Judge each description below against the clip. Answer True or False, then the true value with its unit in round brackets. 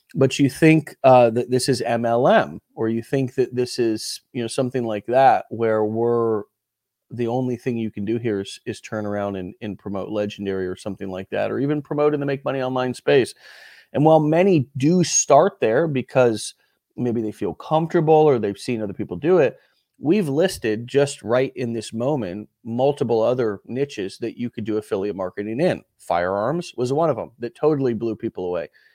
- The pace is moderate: True (195 wpm)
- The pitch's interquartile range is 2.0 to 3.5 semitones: False (4.0 semitones)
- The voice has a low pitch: True (120 Hz)